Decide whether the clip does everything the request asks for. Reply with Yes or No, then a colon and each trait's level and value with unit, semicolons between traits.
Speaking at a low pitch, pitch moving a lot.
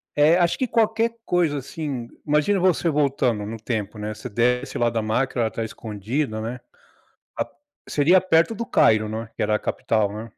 Yes: low, 125 Hz; wide, 7.1 semitones